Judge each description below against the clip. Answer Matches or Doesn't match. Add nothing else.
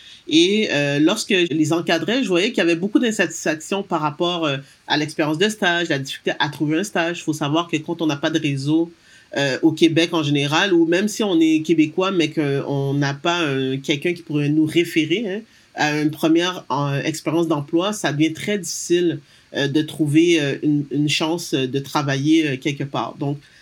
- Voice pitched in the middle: Matches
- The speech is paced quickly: Doesn't match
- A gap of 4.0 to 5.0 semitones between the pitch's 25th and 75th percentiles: Doesn't match